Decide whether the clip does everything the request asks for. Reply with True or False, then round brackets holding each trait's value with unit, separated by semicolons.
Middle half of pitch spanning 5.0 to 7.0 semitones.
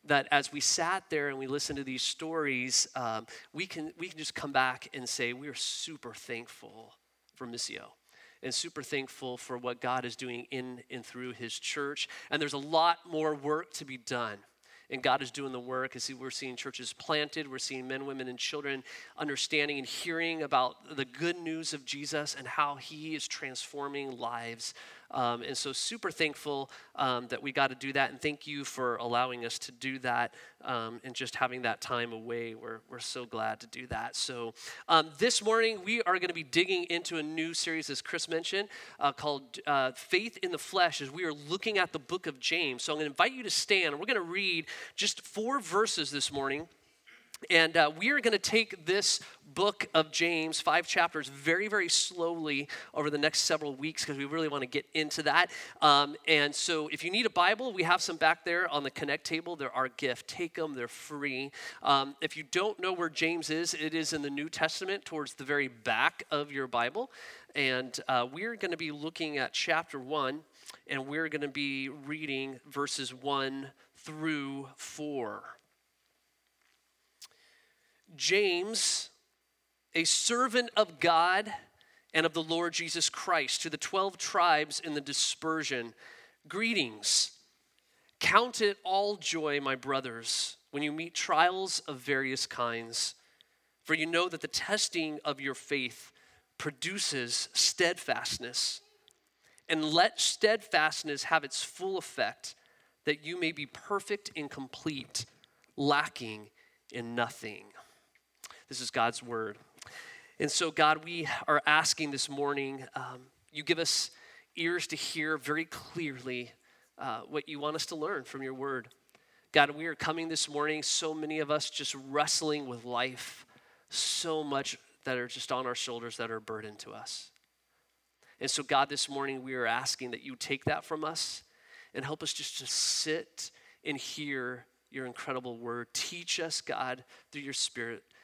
False (3.7 semitones)